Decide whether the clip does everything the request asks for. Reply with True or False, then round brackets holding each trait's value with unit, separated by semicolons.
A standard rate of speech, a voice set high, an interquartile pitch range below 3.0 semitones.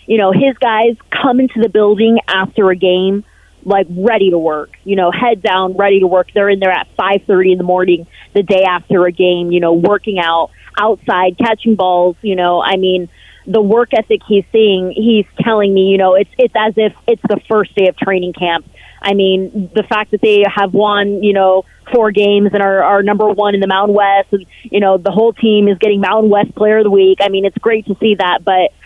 False (230 wpm; 200 Hz; 2.4 semitones)